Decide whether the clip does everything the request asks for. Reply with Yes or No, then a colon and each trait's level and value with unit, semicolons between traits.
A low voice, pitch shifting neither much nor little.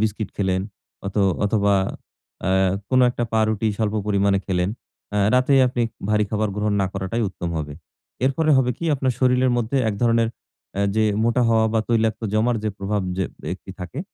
Yes: low, 110 Hz; average, 3.1 semitones